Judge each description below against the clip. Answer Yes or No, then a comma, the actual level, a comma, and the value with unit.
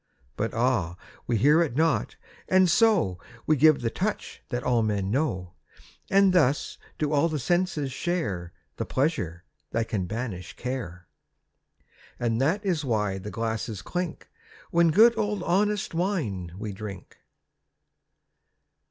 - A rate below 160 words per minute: Yes, slow, 135 wpm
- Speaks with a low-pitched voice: Yes, low, 130 Hz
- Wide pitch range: Yes, wide, 8.4 semitones